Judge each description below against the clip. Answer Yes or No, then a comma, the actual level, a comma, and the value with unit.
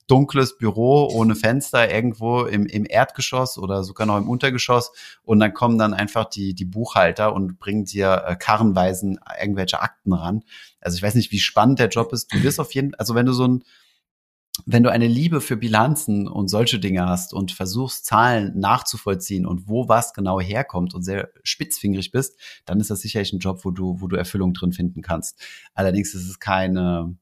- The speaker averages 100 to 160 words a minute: No, fast, 190 wpm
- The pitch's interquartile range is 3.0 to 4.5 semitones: Yes, average, 4.2 semitones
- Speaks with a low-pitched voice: Yes, low, 105 Hz